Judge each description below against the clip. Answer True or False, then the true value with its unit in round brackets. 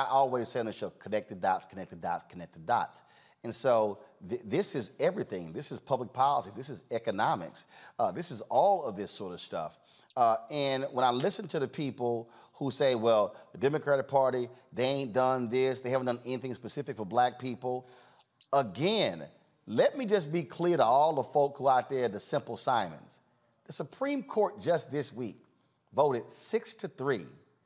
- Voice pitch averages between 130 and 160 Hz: True (135 Hz)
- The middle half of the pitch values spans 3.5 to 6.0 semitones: True (4.4 semitones)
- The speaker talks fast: False (190 wpm)